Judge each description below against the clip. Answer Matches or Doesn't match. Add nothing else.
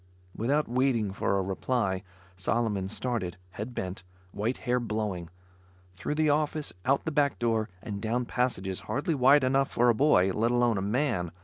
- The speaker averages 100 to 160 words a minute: Doesn't match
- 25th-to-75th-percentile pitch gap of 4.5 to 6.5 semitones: Matches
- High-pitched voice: Doesn't match